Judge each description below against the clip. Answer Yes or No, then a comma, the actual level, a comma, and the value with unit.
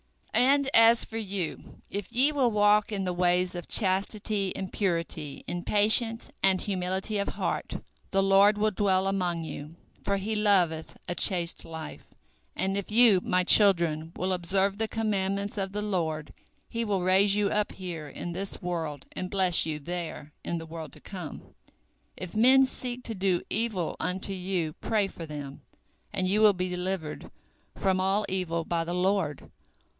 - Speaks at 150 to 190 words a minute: Yes, average, 170 wpm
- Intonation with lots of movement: No, average, 2.9 semitones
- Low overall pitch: No, high, 190 Hz